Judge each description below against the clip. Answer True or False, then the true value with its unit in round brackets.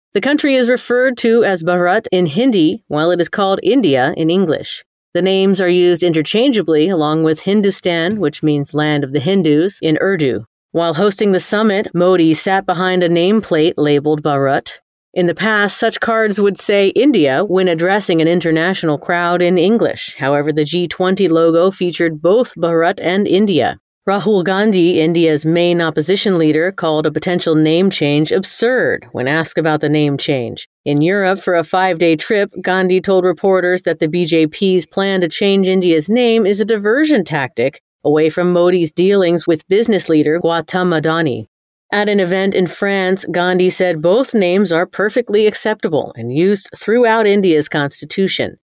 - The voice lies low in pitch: False (180 Hz)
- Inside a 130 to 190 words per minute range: True (165 wpm)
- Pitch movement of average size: True (3.4 semitones)